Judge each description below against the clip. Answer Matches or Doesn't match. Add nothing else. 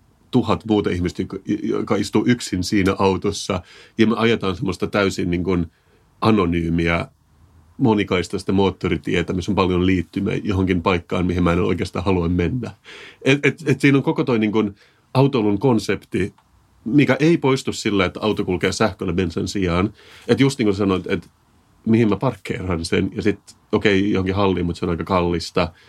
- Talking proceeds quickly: Matches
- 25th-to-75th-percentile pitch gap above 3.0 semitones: Matches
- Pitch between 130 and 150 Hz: Doesn't match